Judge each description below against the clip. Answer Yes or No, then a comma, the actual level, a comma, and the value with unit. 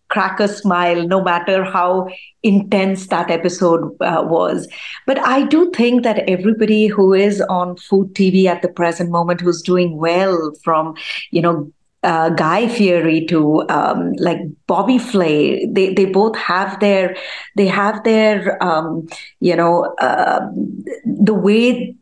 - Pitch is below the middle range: No, medium, 185 Hz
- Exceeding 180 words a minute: No, average, 145 wpm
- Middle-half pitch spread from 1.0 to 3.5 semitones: Yes, average, 3.2 semitones